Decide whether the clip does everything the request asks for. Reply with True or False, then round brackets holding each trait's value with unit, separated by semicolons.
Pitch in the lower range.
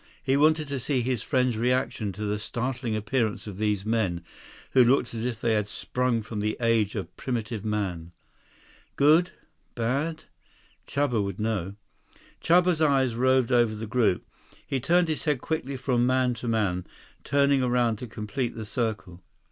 True (120 Hz)